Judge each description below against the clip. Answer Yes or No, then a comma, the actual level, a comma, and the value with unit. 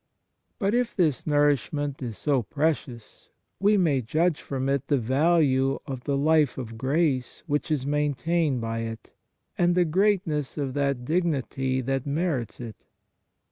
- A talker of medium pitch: Yes, medium, 145 Hz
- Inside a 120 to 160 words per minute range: Yes, average, 145 wpm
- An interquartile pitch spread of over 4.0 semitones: No, average, 3.6 semitones